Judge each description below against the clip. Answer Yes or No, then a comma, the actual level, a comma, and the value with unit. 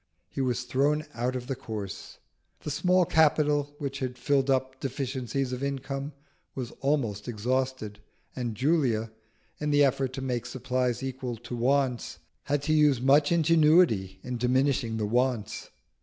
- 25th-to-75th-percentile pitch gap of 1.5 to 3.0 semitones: Yes, average, 2.7 semitones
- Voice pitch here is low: Yes, low, 130 Hz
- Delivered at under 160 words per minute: Yes, average, 150 wpm